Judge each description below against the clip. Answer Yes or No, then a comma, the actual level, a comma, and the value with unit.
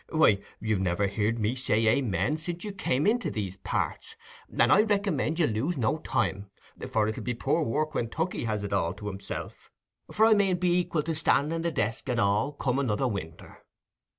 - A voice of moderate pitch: No, low, 125 Hz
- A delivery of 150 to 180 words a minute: No, fast, 205 wpm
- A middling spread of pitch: No, wide, 7.6 semitones